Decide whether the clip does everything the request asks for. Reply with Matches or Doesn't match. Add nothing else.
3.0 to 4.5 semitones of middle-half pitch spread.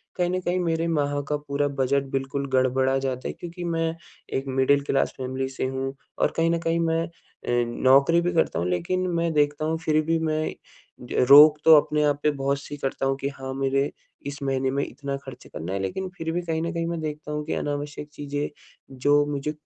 Matches